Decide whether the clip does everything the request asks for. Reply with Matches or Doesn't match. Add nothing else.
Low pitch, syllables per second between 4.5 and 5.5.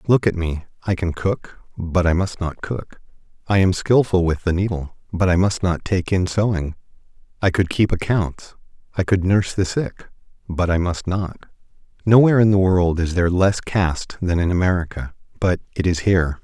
Matches